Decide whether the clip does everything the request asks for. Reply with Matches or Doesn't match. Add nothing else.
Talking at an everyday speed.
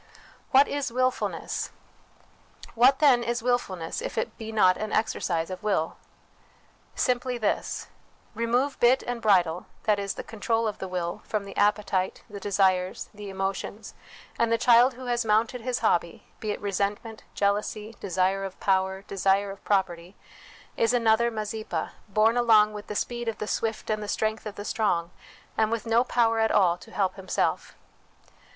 Matches